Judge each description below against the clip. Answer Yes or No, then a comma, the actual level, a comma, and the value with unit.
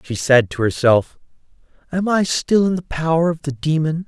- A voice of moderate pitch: Yes, medium, 155 Hz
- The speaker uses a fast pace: No, average, 190 wpm